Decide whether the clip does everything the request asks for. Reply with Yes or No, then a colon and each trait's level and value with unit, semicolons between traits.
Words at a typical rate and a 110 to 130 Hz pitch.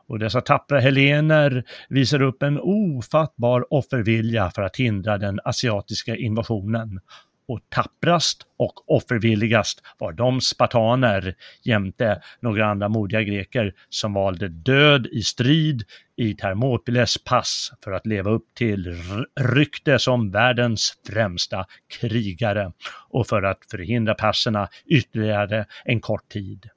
No: slow, 120 wpm; low, 115 Hz